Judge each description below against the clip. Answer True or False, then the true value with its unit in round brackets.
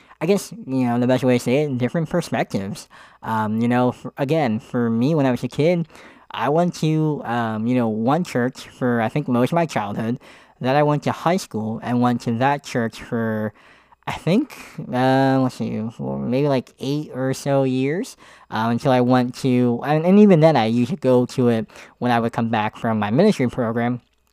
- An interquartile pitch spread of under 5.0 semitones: True (3.4 semitones)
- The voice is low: True (125 Hz)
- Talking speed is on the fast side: True (215 wpm)